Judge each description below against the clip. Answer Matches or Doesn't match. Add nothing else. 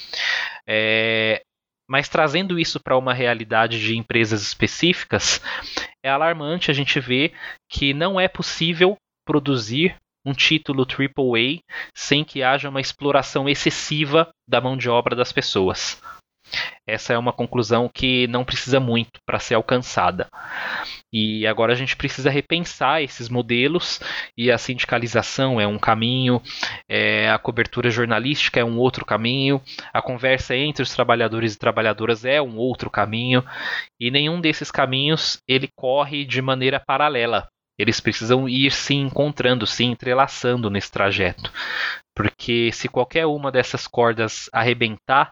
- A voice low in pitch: Matches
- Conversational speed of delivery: Matches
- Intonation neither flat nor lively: Matches